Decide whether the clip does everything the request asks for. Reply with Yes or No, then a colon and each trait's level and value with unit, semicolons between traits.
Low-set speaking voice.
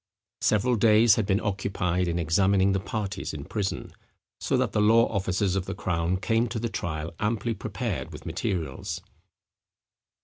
Yes: very low, 95 Hz